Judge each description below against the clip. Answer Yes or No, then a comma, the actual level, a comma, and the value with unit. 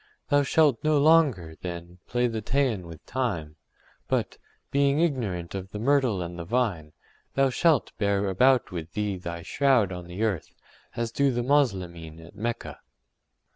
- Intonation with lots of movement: Yes, wide, 7.4 semitones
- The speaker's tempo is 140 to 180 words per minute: Yes, average, 160 wpm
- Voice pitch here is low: Yes, low, 105 Hz